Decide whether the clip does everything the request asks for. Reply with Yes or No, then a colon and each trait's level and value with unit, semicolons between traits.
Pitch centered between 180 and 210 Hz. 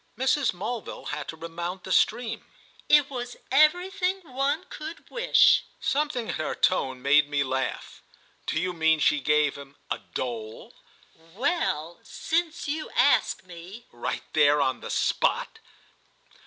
Yes: medium, 185 Hz